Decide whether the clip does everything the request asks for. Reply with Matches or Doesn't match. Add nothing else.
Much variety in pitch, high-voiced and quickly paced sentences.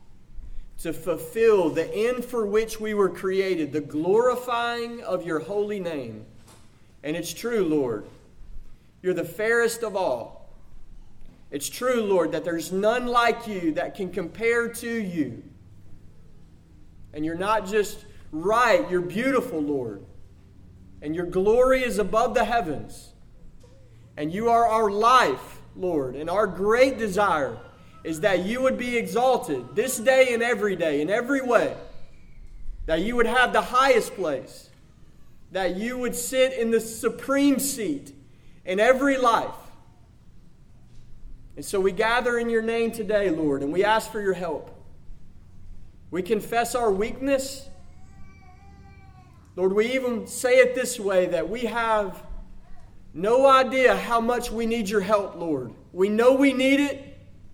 Doesn't match